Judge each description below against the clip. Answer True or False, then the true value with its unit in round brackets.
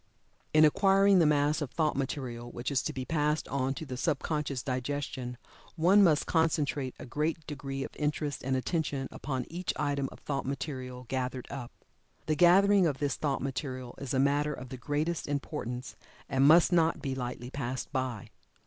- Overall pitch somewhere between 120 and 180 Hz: True (140 Hz)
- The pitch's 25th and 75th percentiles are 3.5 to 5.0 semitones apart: False (2.9 semitones)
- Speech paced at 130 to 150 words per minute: False (180 wpm)